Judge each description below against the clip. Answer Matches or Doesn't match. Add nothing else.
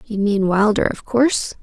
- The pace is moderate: Matches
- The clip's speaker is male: Doesn't match